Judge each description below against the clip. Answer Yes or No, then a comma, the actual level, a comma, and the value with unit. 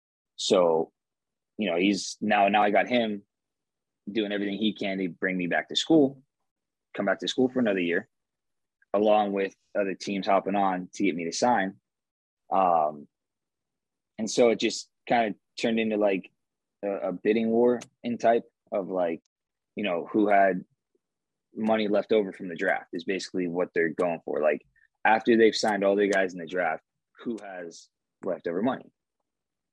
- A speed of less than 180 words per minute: Yes, average, 170 wpm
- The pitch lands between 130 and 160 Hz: No, low, 100 Hz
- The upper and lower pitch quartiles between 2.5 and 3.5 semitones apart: Yes, average, 2.8 semitones